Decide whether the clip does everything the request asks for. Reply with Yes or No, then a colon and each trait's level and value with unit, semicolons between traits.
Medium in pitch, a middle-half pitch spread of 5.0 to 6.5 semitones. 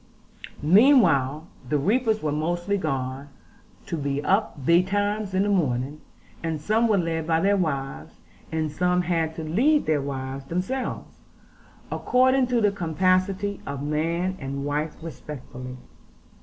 Yes: medium, 165 Hz; wide, 5.6 semitones